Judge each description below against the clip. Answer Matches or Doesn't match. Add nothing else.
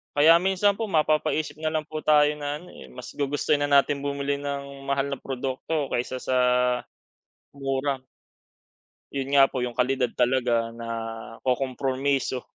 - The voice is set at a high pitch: Doesn't match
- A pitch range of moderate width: Doesn't match